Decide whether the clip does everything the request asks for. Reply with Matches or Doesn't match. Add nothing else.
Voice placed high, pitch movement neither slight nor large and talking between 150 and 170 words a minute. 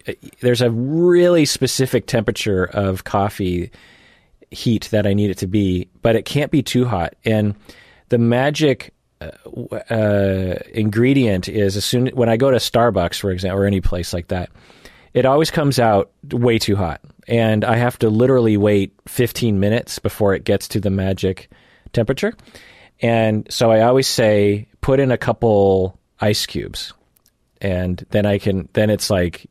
Doesn't match